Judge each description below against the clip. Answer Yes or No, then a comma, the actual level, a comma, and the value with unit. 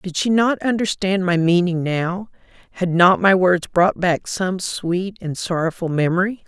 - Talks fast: No, average, 160 wpm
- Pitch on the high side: No, medium, 180 Hz